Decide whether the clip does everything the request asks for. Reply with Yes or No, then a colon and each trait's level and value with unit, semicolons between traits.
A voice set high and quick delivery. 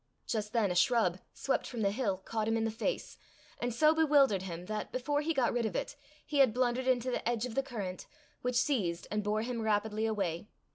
Yes: high, 225 Hz; fast, 225 wpm